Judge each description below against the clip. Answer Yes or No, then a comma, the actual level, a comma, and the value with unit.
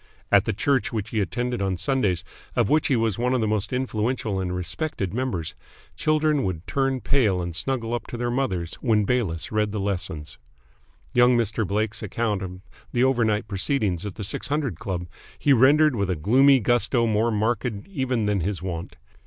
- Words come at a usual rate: Yes, average, 185 wpm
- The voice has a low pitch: Yes, low, 110 Hz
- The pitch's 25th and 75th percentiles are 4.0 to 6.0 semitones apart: Yes, average, 4.7 semitones